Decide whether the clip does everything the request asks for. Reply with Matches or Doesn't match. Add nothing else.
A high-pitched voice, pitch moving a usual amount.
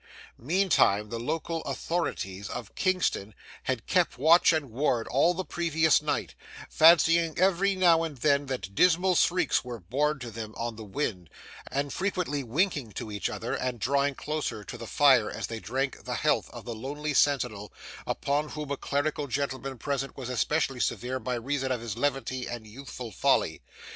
Doesn't match